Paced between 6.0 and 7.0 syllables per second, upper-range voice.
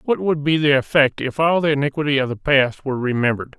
No: 6.3 syllables/s; medium, 140 Hz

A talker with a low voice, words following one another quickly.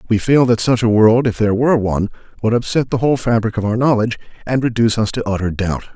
Yes: low, 115 Hz; fast, 240 wpm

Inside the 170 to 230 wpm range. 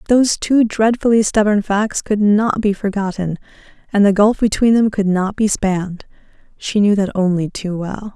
Yes: average, 175 wpm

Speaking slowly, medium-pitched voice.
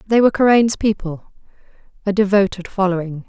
No: slow, 110 wpm; high, 195 Hz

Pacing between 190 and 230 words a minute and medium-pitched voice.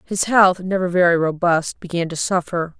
No: average, 170 wpm; medium, 175 Hz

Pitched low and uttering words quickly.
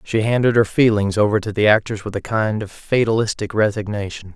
No: low, 105 Hz; average, 195 wpm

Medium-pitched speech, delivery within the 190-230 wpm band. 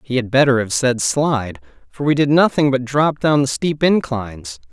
No: low, 130 Hz; fast, 205 wpm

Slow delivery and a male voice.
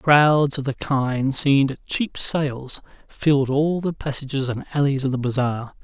No: average, 175 wpm; male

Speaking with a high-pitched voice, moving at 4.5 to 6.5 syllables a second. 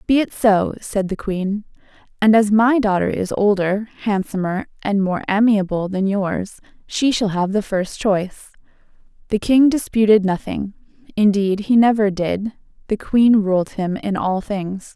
No: high, 205 Hz; 4.3 syllables/s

